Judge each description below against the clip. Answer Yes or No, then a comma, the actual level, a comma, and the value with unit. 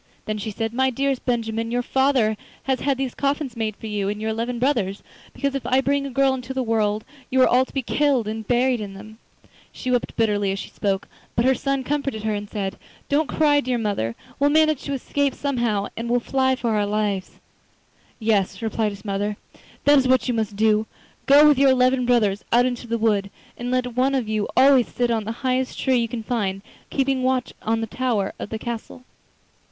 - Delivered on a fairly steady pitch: No, average, 3.5 semitones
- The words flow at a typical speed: No, fast, 215 wpm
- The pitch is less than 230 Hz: No, high, 240 Hz